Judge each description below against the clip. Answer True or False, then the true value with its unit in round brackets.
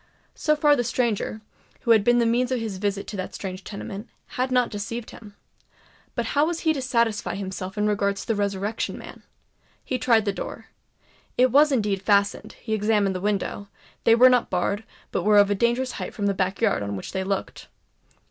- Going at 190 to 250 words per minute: True (200 wpm)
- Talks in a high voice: True (215 Hz)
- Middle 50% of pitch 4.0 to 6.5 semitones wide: False (3.3 semitones)